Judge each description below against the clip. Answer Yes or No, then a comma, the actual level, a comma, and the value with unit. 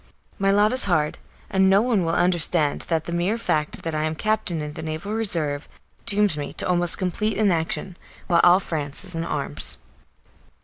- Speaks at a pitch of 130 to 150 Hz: No, medium, 175 Hz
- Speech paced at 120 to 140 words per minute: No, average, 190 wpm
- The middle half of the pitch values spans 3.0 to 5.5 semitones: Yes, average, 4.1 semitones